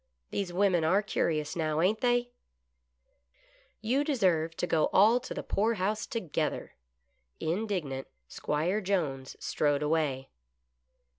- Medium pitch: Yes, medium, 175 Hz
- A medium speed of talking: No, slow, 125 wpm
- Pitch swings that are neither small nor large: No, wide, 5.8 semitones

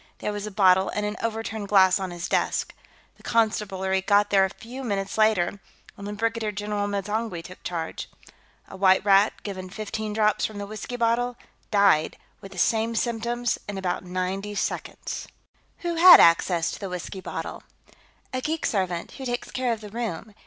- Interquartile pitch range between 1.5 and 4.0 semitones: Yes, average, 2.8 semitones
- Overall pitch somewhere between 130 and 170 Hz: No, high, 205 Hz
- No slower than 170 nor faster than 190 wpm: Yes, average, 180 wpm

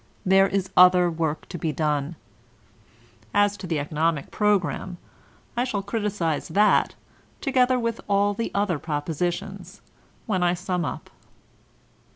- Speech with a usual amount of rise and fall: Yes, average, 3.7 semitones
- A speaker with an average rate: No, slow, 130 wpm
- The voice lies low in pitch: No, medium, 185 Hz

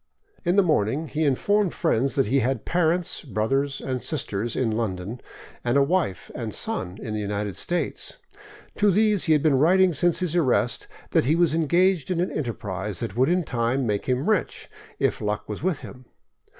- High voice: No, medium, 140 Hz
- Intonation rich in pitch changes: Yes, wide, 7.3 semitones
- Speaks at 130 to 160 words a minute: No, average, 190 wpm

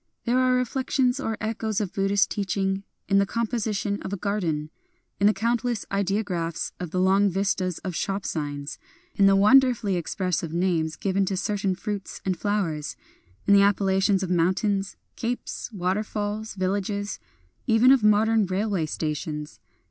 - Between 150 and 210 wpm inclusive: Yes, average, 165 wpm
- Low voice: No, high, 200 Hz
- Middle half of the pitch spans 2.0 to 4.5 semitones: Yes, narrow, 2.6 semitones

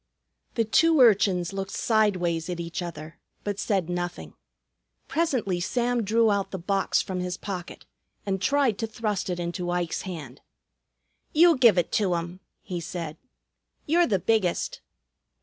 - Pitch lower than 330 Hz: Yes, high, 190 Hz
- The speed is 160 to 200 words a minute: No, average, 150 wpm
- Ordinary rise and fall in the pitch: Yes, average, 4.1 semitones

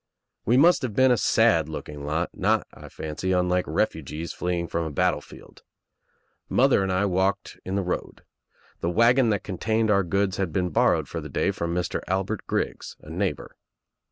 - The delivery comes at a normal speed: Yes, average, 180 wpm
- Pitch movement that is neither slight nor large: Yes, average, 4.1 semitones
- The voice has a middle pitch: No, very low, 95 Hz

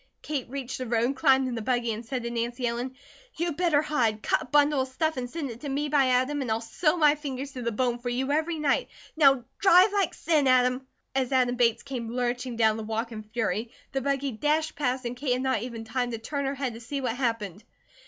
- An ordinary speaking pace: No, fast, 240 wpm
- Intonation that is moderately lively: Yes, average, 3.1 semitones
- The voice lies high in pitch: Yes, very high, 255 Hz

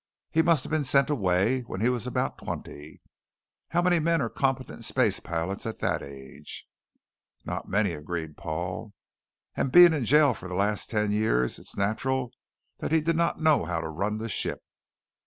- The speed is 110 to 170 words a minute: No, average, 180 wpm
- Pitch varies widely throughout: Yes, wide, 8.0 semitones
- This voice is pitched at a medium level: No, low, 110 Hz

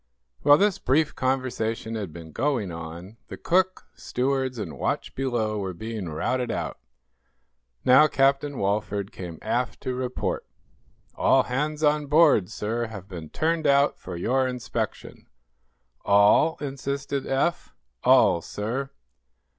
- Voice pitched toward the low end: Yes, low, 125 Hz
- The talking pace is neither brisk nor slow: No, slow, 130 wpm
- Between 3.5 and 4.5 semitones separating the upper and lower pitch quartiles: No, average, 5.3 semitones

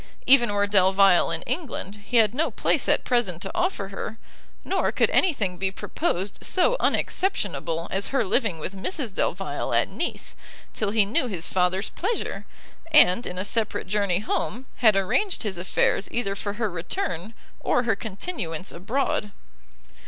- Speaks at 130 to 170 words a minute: Yes, average, 160 wpm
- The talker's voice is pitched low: No, high, 205 Hz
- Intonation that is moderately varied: Yes, average, 4.3 semitones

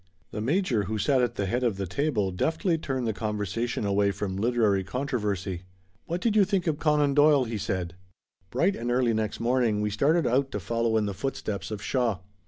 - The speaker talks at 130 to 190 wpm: No, average, 200 wpm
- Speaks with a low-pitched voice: Yes, low, 115 Hz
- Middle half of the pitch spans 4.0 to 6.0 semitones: Yes, average, 5.2 semitones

